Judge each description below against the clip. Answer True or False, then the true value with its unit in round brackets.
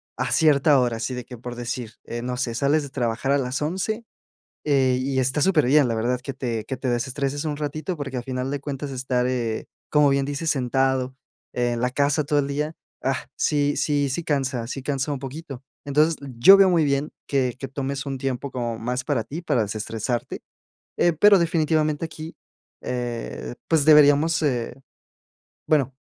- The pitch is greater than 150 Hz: False (135 Hz)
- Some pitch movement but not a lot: True (3.1 semitones)